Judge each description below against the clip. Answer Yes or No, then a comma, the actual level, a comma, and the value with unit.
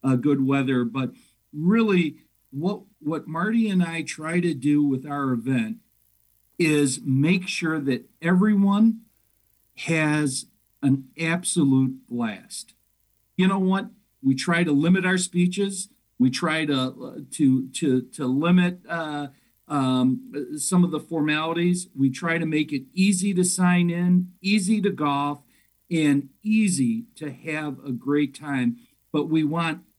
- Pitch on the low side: No, medium, 155 Hz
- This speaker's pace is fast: No, average, 140 wpm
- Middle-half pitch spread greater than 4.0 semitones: Yes, average, 5.1 semitones